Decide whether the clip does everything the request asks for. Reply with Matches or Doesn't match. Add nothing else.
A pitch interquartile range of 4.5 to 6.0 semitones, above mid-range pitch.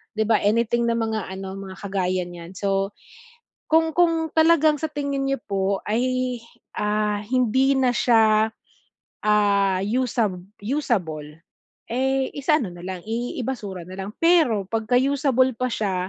Matches